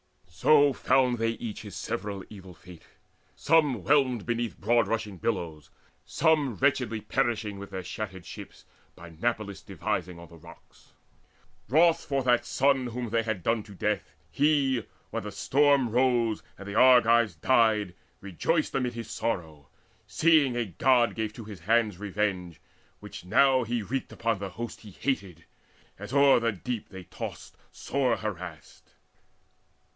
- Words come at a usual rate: Yes, average, 150 wpm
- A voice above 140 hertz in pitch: No, low, 115 Hz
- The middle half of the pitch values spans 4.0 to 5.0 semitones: Yes, average, 4.6 semitones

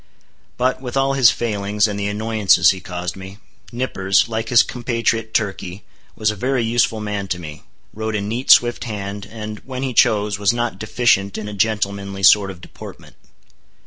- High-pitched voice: No, low, 105 Hz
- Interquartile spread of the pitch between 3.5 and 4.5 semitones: No, average, 2.9 semitones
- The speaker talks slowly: No, average, 175 wpm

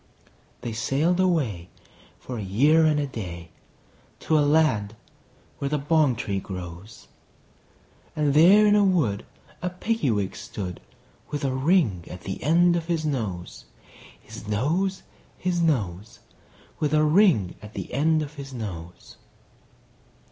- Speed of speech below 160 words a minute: Yes, average, 140 wpm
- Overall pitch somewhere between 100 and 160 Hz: Yes, medium, 140 Hz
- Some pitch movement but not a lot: No, wide, 7.7 semitones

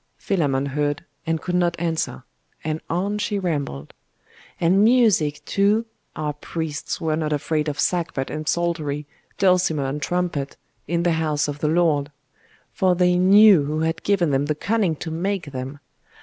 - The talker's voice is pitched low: No, medium, 160 Hz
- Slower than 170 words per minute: Yes, average, 160 wpm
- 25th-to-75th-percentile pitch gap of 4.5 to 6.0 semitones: No, average, 3.4 semitones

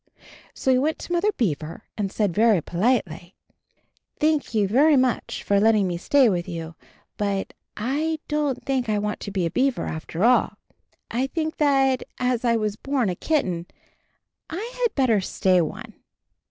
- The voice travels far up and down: Yes, wide, 6.0 semitones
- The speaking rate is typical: Yes, average, 170 wpm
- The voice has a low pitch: No, high, 230 Hz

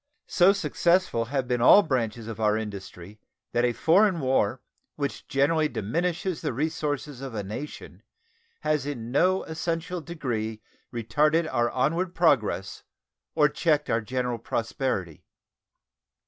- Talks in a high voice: No, low, 135 Hz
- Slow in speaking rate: Yes, slow, 130 wpm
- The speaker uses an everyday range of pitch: No, wide, 6.0 semitones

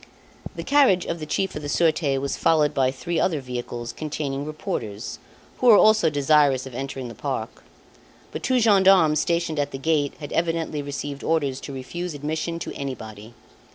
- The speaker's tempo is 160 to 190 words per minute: Yes, average, 175 wpm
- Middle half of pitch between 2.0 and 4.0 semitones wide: Yes, average, 3.7 semitones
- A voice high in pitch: No, medium, 150 Hz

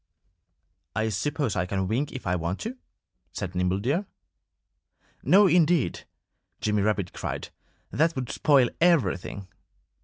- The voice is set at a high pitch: No, low, 110 Hz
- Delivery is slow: Yes, slow, 125 wpm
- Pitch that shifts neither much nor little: No, wide, 8.3 semitones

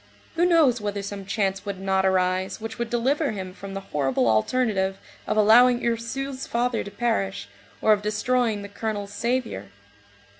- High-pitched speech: Yes, high, 210 Hz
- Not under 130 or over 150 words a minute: No, average, 160 wpm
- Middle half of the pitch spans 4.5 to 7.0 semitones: No, average, 3.8 semitones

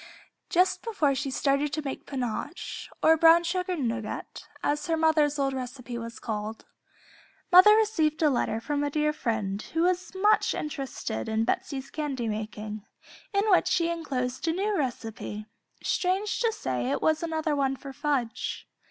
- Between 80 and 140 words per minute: No, average, 160 wpm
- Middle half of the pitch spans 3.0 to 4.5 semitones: No, wide, 5.6 semitones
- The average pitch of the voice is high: Yes, very high, 290 Hz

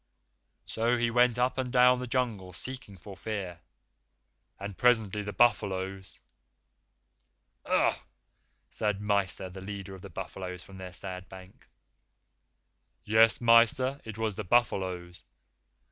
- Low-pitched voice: Yes, low, 105 Hz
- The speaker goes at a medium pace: No, slow, 130 wpm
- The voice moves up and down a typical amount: Yes, average, 4.0 semitones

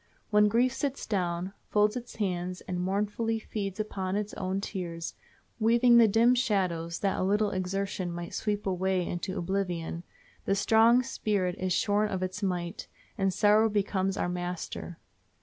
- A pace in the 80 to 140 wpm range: No, average, 155 wpm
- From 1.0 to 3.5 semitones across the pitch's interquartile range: Yes, average, 2.8 semitones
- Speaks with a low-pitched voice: No, high, 195 Hz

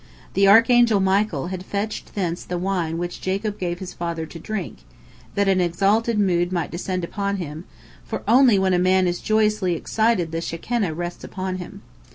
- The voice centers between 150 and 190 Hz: Yes, medium, 185 Hz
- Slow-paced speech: No, average, 180 wpm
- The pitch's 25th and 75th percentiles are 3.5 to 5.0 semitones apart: No, average, 3.0 semitones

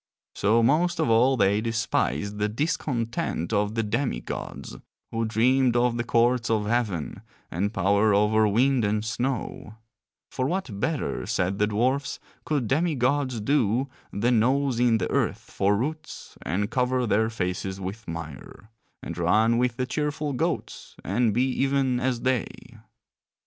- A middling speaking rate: Yes, average, 150 wpm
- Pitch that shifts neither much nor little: Yes, average, 3.8 semitones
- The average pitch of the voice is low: Yes, low, 115 Hz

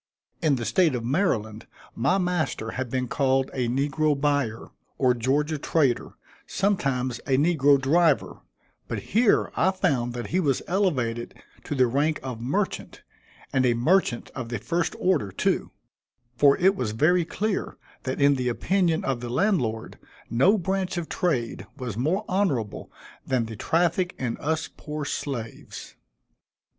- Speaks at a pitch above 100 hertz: Yes, medium, 140 Hz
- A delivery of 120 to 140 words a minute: No, average, 150 wpm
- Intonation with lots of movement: Yes, wide, 6.1 semitones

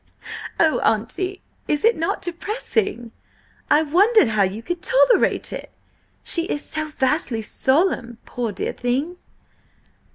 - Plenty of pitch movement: Yes, wide, 7.5 semitones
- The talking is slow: Yes, slow, 125 wpm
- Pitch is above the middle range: Yes, very high, 310 Hz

